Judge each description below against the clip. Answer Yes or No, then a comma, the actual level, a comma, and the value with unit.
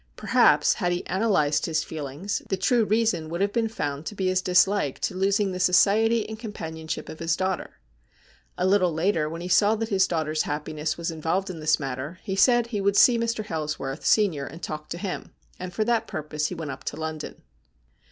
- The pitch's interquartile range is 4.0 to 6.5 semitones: Yes, average, 4.6 semitones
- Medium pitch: Yes, medium, 180 Hz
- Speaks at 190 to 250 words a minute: Yes, fast, 205 wpm